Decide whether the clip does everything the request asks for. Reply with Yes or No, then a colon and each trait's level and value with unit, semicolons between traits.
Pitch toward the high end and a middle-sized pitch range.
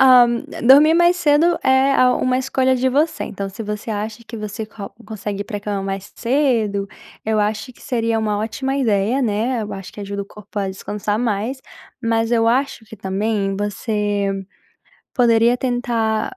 Yes: high, 225 Hz; average, 3.6 semitones